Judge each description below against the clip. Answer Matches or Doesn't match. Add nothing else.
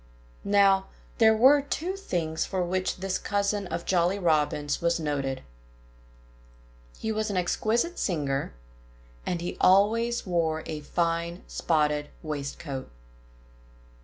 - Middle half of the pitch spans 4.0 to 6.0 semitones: Matches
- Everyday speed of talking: Doesn't match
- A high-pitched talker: Doesn't match